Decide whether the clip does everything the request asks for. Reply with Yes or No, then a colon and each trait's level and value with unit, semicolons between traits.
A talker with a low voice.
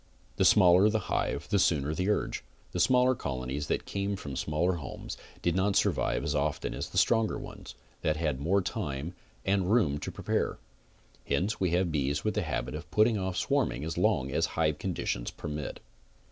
Yes: very low, 85 Hz